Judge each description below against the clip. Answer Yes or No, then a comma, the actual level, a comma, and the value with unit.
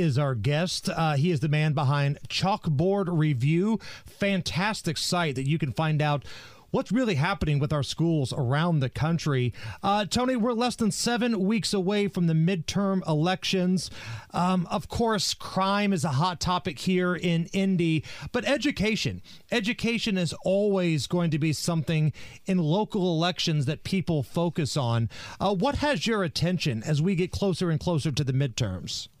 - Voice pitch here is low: No, medium, 170 Hz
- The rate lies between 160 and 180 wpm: Yes, average, 165 wpm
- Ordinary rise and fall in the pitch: Yes, average, 4.6 semitones